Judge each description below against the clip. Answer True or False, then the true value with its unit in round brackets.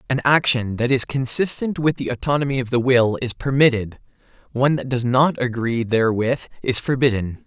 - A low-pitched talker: True (125 Hz)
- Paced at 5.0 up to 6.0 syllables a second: True (5.4 syllables/s)